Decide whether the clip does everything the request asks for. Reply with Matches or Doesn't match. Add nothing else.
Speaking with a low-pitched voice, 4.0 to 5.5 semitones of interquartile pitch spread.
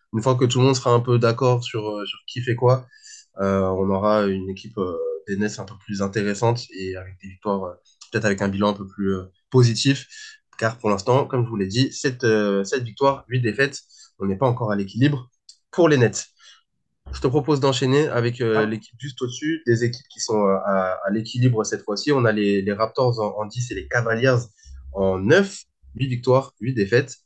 Matches